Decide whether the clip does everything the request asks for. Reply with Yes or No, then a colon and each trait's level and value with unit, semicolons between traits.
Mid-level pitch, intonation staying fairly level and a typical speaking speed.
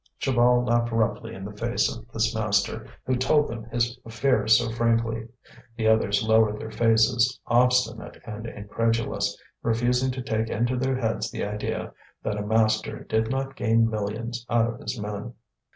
No: low, 115 Hz; narrow, 1.6 semitones; average, 165 wpm